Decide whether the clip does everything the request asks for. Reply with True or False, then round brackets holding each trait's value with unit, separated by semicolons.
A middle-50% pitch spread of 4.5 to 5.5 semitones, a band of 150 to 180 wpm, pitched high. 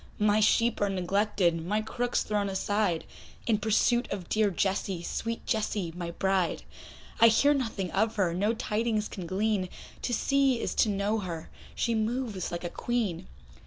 False (3.2 semitones; 160 wpm; 210 Hz)